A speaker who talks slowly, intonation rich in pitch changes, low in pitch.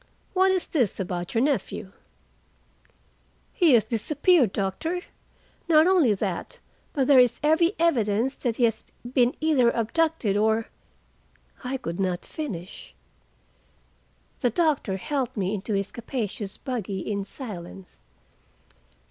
No: slow, 125 wpm; wide, 7.1 semitones; high, 235 Hz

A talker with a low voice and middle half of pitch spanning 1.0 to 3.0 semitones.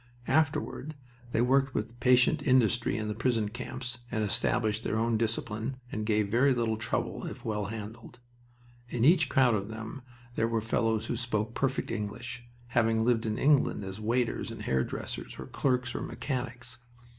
Yes: low, 115 Hz; narrow, 2.5 semitones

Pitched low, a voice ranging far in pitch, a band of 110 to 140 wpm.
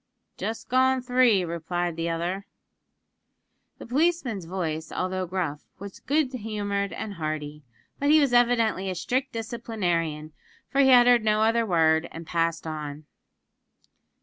No: high, 200 Hz; wide, 6.6 semitones; slow, 135 wpm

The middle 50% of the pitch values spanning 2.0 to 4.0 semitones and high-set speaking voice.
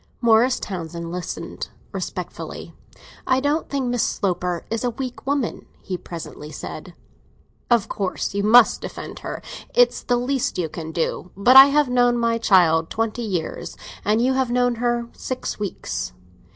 No: wide, 5.4 semitones; high, 230 Hz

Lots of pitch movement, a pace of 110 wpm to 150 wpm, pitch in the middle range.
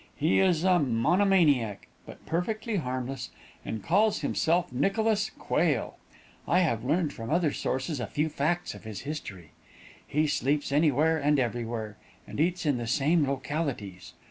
Yes: wide, 5.8 semitones; average, 145 wpm; medium, 150 Hz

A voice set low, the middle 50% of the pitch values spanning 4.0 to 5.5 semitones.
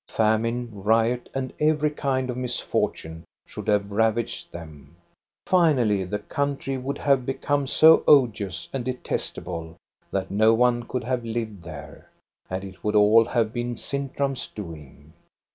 Yes: low, 115 Hz; average, 4.6 semitones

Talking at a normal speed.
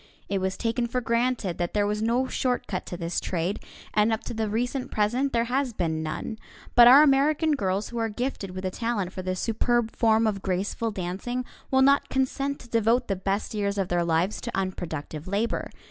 No: fast, 210 wpm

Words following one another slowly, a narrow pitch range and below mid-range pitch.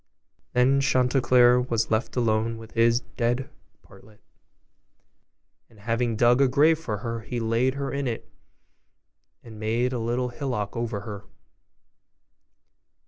Yes: slow, 130 wpm; narrow, 2.1 semitones; low, 120 Hz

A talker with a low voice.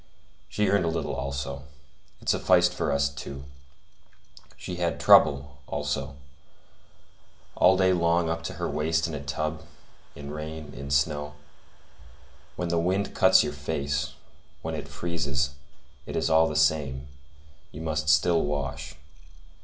Yes: very low, 75 Hz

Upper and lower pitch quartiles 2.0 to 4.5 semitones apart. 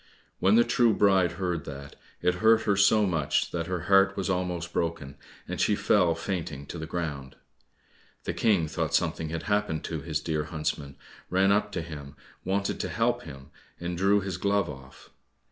Yes: average, 4.2 semitones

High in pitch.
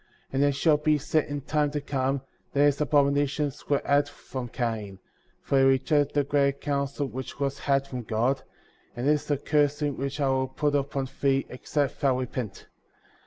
No: medium, 140 Hz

